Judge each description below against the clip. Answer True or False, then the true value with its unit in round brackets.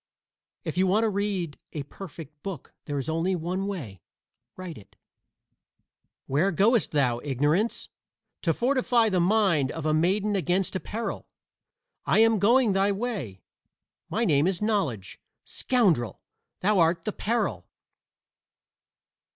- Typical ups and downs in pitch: False (5.7 semitones)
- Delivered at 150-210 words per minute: False (135 wpm)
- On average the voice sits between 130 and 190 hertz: True (185 Hz)